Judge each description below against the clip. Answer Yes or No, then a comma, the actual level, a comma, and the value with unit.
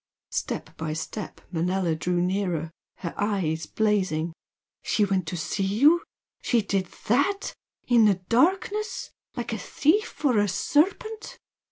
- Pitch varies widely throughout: Yes, wide, 7.2 semitones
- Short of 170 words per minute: Yes, slow, 135 wpm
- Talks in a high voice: Yes, high, 205 Hz